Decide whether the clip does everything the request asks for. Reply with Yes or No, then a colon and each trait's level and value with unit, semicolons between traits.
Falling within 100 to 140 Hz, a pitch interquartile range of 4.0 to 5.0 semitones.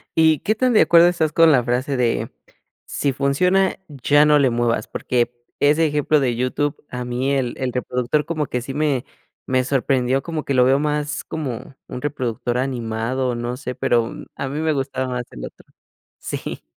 No: low, 135 Hz; average, 3.2 semitones